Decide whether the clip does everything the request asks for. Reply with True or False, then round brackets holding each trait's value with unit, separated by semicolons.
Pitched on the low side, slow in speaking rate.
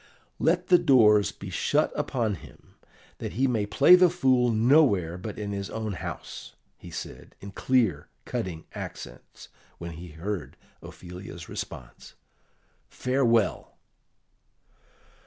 True (105 Hz; 120 wpm)